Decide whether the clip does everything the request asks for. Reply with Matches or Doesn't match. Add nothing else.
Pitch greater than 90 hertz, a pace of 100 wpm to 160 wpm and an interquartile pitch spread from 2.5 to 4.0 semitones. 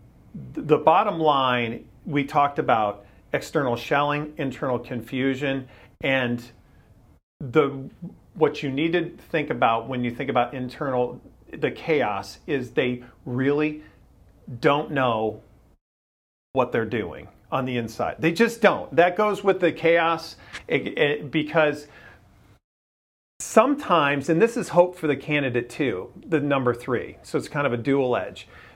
Doesn't match